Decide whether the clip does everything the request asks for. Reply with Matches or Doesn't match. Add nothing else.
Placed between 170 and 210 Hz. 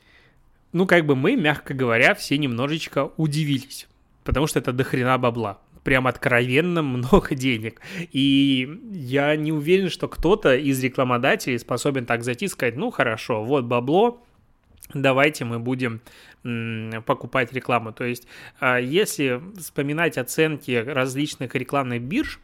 Doesn't match